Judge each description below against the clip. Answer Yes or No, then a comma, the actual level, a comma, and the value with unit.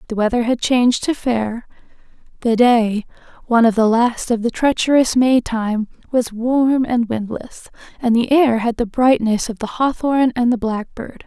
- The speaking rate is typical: Yes, average, 175 wpm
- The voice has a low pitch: No, high, 235 Hz